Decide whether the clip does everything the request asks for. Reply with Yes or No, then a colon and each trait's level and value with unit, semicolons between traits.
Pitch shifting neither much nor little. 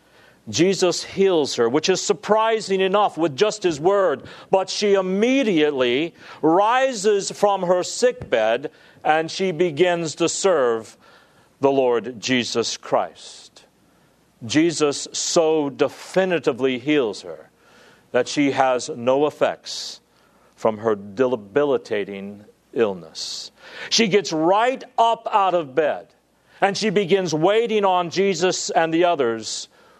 No: wide, 6.1 semitones